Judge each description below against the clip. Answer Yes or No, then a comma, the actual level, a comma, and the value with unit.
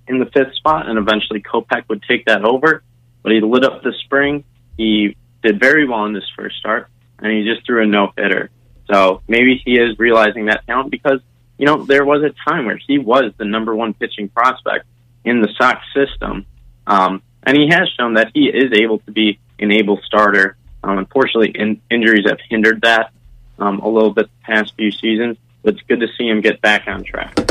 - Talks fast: Yes, fast, 210 wpm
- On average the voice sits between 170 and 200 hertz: No, low, 115 Hz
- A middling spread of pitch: Yes, average, 3.2 semitones